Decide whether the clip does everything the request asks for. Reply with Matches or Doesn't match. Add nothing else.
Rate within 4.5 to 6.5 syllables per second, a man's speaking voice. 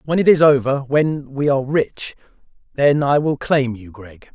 Matches